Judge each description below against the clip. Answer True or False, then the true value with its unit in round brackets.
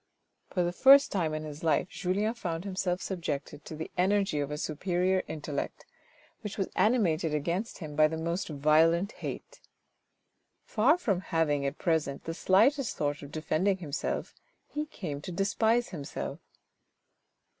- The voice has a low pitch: False (170 Hz)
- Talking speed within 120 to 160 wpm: True (150 wpm)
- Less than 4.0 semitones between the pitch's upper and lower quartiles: False (4.3 semitones)